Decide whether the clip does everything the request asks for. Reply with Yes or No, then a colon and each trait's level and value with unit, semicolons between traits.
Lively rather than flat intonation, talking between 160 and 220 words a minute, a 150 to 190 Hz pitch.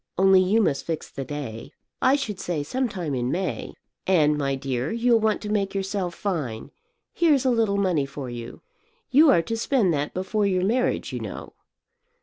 Yes: wide, 6.9 semitones; average, 185 wpm; medium, 185 Hz